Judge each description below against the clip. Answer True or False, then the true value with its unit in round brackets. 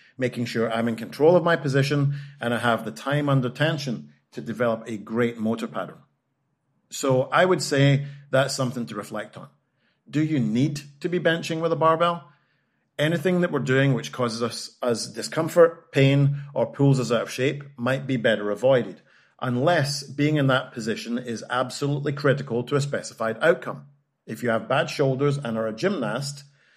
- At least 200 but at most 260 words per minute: False (180 wpm)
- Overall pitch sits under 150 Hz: True (135 Hz)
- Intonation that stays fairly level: False (3.3 semitones)